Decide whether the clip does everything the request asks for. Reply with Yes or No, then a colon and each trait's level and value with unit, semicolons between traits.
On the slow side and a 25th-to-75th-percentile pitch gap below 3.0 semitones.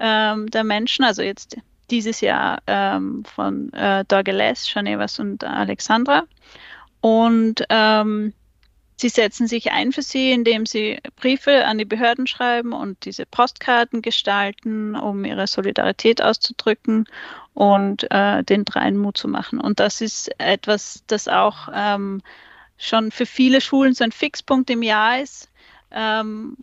No: average, 135 wpm; narrow, 2.5 semitones